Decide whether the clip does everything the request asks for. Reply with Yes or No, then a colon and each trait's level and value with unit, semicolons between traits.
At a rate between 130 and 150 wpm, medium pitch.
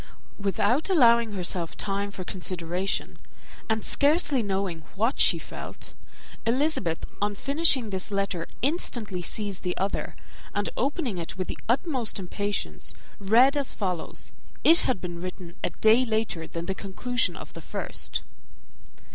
No: average, 140 wpm; high, 205 Hz